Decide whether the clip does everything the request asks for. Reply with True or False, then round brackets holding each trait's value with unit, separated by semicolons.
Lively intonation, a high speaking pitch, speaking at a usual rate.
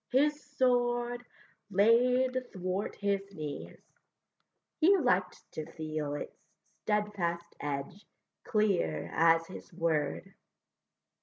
False (6.6 semitones; 195 Hz; 90 wpm)